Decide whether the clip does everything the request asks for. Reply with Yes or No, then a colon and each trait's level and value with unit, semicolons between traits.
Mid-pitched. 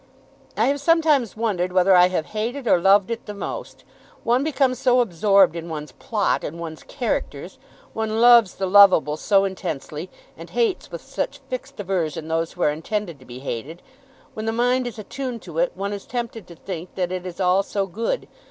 No: high, 200 Hz